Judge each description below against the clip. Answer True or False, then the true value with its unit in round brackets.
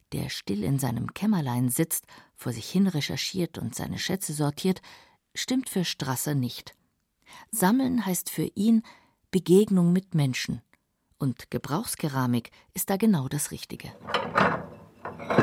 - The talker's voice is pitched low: False (175 Hz)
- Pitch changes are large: True (6.6 semitones)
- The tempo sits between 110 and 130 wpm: True (125 wpm)